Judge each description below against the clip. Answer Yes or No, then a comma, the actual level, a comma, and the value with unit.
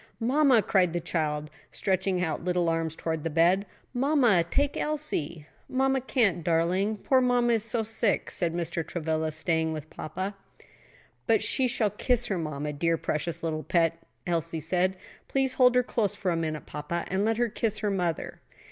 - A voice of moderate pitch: Yes, medium, 180 Hz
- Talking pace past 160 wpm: Yes, average, 175 wpm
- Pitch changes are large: Yes, wide, 5.9 semitones